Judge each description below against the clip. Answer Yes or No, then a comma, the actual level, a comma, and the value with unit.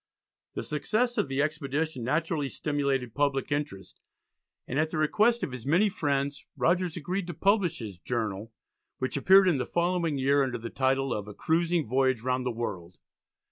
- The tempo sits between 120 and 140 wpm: No, average, 175 wpm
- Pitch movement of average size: Yes, average, 4.8 semitones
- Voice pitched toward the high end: No, medium, 140 Hz